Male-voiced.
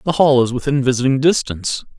Yes: male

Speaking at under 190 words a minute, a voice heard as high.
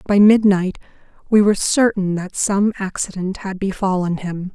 Yes: average, 145 wpm; high, 195 Hz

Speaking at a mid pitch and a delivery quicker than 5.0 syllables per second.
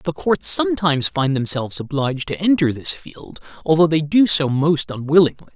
Yes: medium, 160 Hz; 5.5 syllables/s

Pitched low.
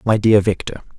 Yes: low, 105 Hz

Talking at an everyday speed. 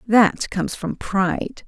Yes: average, 145 wpm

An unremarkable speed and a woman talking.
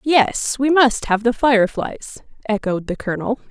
Yes: average, 155 wpm; female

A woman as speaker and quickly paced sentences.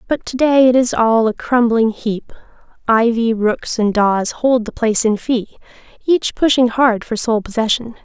No: female; average, 170 wpm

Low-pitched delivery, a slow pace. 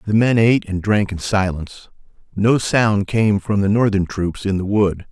No: low, 100 Hz; average, 200 wpm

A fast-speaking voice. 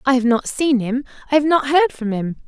Yes: fast, 265 wpm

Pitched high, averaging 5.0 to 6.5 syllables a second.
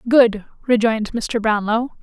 No: high, 225 Hz; 4.4 syllables/s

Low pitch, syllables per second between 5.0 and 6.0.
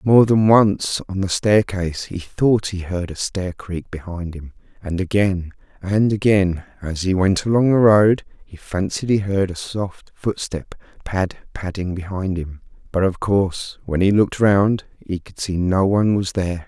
No: very low, 95 Hz; 4.4 syllables/s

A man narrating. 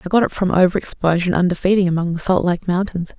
No: female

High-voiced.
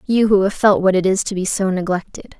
Yes: high, 195 Hz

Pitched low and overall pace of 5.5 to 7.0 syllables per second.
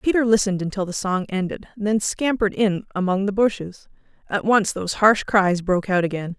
No: high, 200 Hz; 5.6 syllables/s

